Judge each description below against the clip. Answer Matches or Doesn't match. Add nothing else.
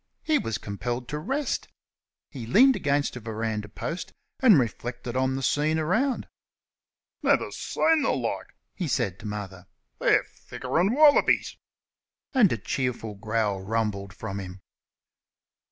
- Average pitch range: Doesn't match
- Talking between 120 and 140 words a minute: Matches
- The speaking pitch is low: Matches